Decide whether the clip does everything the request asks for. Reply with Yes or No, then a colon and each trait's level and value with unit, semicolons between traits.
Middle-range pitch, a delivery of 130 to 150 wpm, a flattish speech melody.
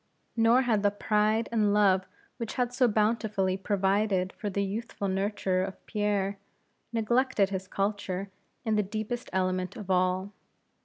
No: high, 205 Hz; average, 145 wpm; narrow, 2.3 semitones